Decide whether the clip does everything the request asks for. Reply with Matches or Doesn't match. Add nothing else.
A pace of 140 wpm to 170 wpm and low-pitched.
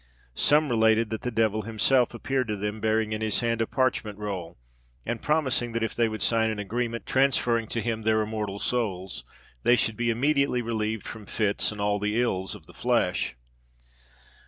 Doesn't match